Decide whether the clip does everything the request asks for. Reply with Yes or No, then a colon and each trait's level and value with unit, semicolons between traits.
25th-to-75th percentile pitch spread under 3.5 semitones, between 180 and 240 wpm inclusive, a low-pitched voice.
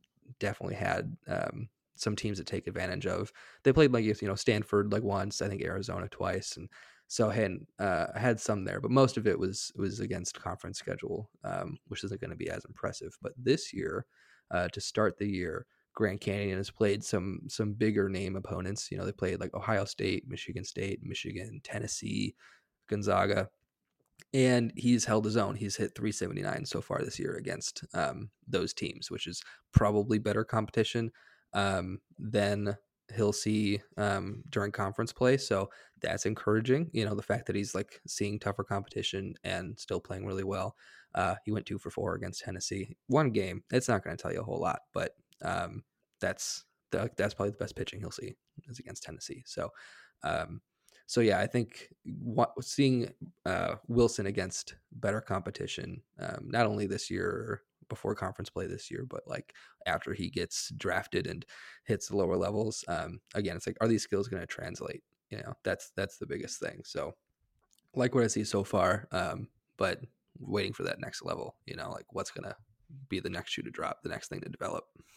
Yes: average, 2.8 semitones; average, 190 wpm; low, 105 Hz